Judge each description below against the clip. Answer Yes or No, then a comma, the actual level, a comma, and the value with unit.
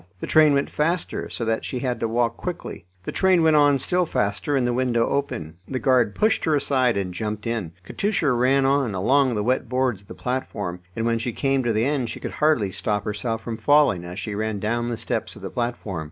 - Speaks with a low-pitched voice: Yes, low, 120 Hz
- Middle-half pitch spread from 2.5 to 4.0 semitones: No, average, 4.4 semitones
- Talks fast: Yes, fast, 230 wpm